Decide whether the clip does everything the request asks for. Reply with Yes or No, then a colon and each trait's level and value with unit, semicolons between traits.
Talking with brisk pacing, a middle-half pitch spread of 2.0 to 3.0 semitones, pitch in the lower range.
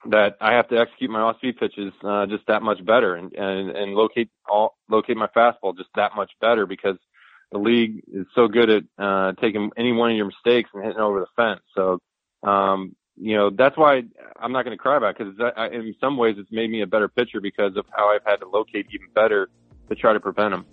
Yes: fast, 235 wpm; narrow, 2.6 semitones; low, 105 Hz